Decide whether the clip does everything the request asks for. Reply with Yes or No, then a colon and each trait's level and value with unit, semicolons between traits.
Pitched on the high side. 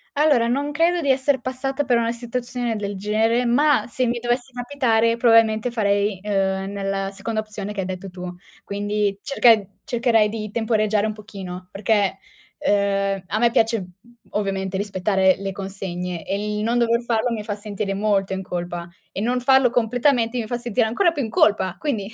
Yes: high, 215 Hz